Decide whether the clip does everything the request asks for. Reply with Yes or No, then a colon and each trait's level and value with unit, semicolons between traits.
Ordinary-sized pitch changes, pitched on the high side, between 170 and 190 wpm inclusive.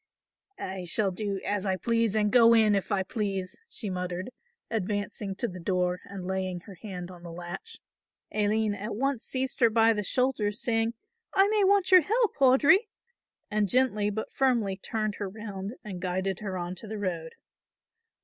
Yes: average, 3.5 semitones; high, 210 Hz; average, 180 wpm